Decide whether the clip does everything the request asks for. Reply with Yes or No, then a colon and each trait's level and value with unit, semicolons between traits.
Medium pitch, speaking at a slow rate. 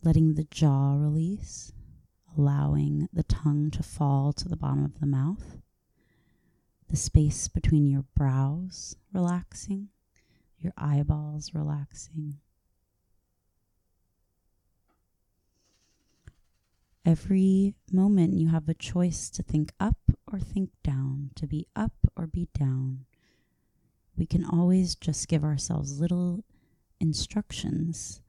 Yes: medium, 145 Hz; slow, 105 wpm